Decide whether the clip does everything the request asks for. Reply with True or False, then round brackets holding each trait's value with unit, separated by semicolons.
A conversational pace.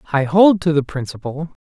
True (185 wpm)